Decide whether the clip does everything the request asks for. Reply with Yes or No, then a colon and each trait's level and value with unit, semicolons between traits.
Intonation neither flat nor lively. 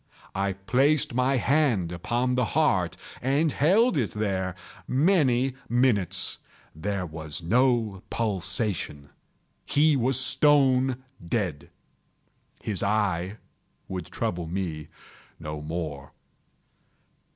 No: wide, 6.6 semitones